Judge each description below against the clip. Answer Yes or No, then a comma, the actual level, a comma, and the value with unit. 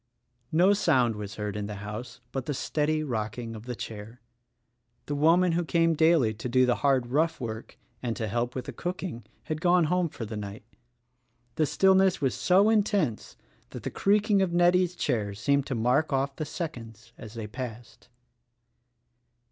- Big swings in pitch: Yes, wide, 6.8 semitones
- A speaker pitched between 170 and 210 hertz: No, low, 130 Hz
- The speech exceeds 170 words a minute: Yes, average, 185 wpm